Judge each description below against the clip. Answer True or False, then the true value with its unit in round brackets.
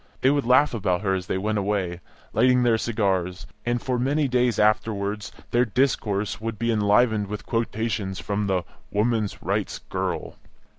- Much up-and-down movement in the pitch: False (3.2 semitones)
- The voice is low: True (110 Hz)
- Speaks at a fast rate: False (160 wpm)